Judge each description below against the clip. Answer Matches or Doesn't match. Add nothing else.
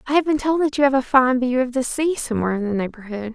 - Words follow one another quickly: Matches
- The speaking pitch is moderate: Doesn't match